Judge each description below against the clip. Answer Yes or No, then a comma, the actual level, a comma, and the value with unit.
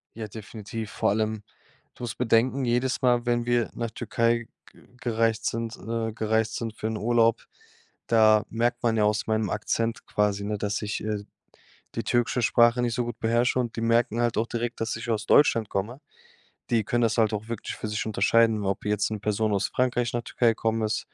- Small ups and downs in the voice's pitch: Yes, narrow, 1.6 semitones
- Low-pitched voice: Yes, low, 115 Hz